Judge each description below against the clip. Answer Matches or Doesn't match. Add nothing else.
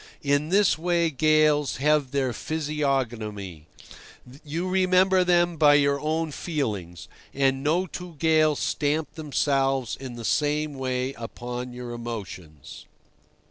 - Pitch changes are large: Doesn't match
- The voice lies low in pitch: Doesn't match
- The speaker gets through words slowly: Matches